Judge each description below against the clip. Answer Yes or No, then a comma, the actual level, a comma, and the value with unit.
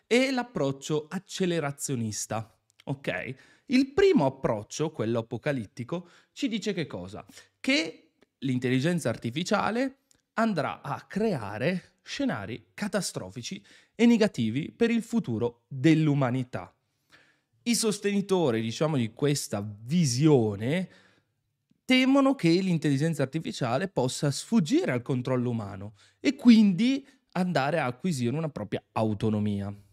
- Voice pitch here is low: No, medium, 155 Hz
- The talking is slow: Yes, slow, 100 wpm